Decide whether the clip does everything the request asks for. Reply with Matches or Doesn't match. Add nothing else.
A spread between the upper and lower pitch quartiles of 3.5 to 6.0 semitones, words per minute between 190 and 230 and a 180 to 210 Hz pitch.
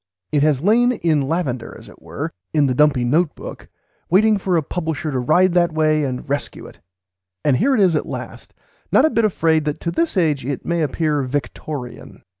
Doesn't match